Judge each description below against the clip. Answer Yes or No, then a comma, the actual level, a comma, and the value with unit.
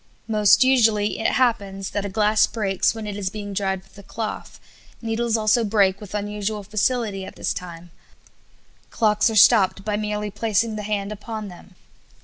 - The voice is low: No, high, 210 Hz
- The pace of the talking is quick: No, average, 170 wpm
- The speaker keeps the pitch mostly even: Yes, narrow, 1.9 semitones